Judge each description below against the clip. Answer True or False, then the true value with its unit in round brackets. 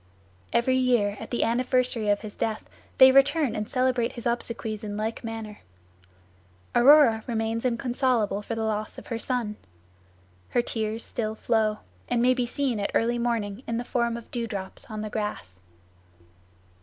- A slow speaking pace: False (165 wpm)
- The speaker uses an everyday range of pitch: False (2.3 semitones)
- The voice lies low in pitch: False (230 Hz)